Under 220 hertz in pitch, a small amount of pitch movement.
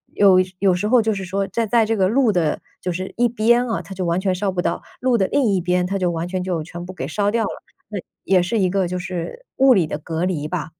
No: high, 190 Hz; average, 3.5 semitones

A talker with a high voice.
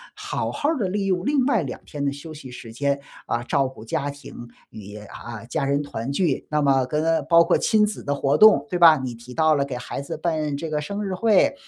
No: medium, 145 Hz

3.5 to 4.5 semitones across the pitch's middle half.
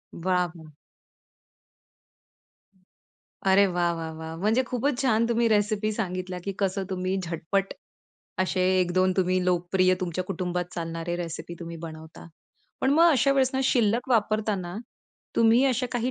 Yes: average, 4.2 semitones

